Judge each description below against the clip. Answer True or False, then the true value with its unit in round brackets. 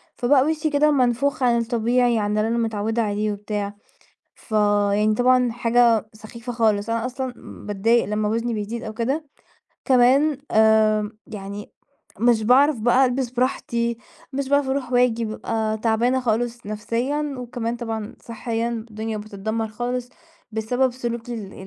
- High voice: True (230 Hz)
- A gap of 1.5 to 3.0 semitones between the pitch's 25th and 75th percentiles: True (2.4 semitones)